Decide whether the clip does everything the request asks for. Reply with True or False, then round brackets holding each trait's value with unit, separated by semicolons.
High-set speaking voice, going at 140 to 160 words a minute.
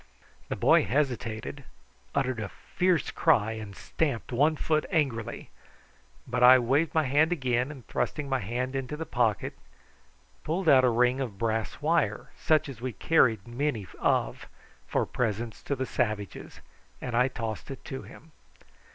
False (130 Hz; 155 wpm)